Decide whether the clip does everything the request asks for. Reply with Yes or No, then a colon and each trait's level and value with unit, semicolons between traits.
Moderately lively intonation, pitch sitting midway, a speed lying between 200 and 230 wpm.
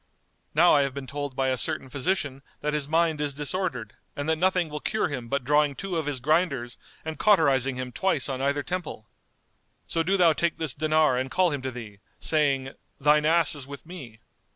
Yes: average, 3.5 semitones; medium, 145 Hz; fast, 205 wpm